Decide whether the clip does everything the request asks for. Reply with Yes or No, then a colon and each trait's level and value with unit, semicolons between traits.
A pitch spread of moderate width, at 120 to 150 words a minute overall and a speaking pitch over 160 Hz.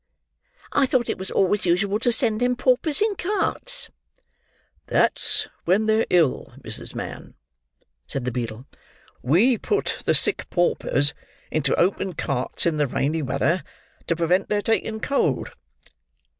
No: wide, 7.9 semitones; average, 140 wpm; high, 190 Hz